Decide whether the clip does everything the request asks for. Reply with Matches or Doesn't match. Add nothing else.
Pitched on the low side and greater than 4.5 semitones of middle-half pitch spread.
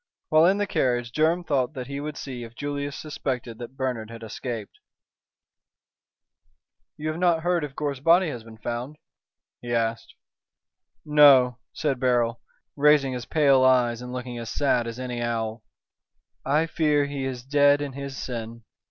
Doesn't match